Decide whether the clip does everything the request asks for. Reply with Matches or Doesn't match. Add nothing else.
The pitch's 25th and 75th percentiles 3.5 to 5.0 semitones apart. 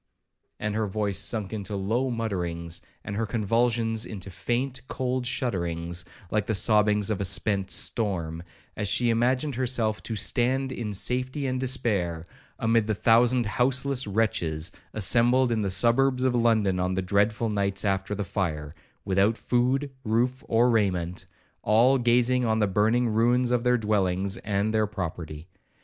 Matches